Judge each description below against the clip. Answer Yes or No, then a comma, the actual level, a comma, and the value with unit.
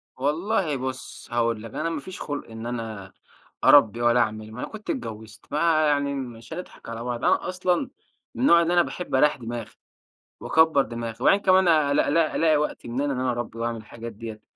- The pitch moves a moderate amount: No, wide, 5.7 semitones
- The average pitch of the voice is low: Yes, low, 130 Hz